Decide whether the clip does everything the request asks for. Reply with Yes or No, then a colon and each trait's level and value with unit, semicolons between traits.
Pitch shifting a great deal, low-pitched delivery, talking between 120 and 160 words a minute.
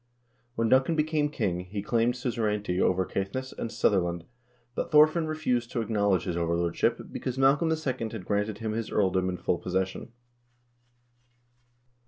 Yes: wide, 5.9 semitones; low, 110 Hz; average, 150 wpm